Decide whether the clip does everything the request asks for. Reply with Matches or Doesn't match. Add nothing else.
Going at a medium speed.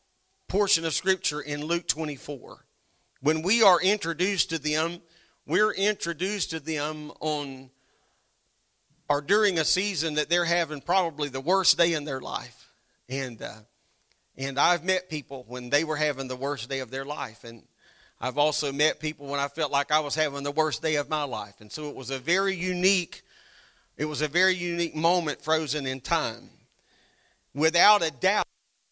Matches